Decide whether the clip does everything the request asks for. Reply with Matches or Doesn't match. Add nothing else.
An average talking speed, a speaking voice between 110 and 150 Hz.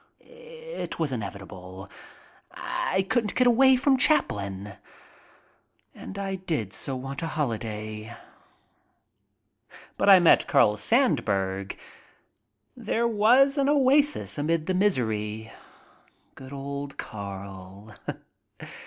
Doesn't match